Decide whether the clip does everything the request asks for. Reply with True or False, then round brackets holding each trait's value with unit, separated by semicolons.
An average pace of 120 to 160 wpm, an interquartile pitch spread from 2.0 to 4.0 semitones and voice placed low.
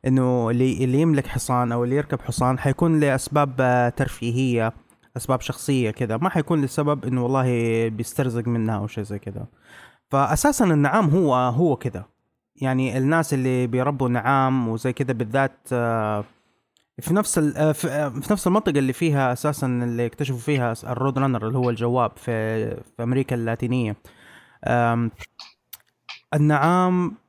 True (130 wpm; 3.4 semitones; 130 Hz)